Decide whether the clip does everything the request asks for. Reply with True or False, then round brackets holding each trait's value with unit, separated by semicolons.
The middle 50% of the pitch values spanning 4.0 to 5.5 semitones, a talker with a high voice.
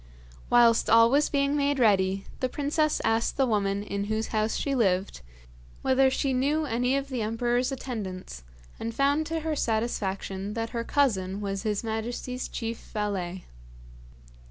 True (4.7 semitones; 230 Hz)